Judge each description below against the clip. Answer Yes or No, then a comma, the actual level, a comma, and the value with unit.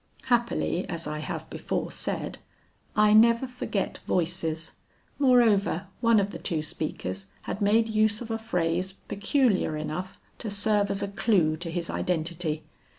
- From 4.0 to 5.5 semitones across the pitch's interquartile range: Yes, average, 4.8 semitones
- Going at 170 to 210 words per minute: No, average, 150 wpm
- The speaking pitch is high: Yes, high, 195 Hz